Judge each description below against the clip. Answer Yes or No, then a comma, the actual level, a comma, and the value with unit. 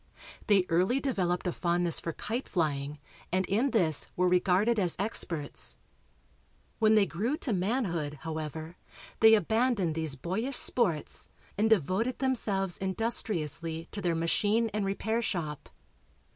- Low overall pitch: No, medium, 185 Hz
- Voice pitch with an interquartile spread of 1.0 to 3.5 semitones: No, average, 5.0 semitones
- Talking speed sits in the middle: No, slow, 130 wpm